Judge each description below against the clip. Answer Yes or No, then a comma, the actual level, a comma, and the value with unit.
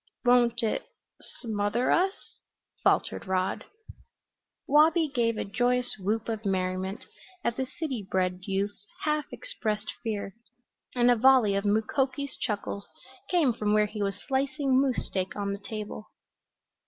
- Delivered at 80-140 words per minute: Yes, slow, 135 wpm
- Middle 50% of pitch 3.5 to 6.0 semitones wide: Yes, average, 4.5 semitones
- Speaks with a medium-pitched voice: No, high, 220 Hz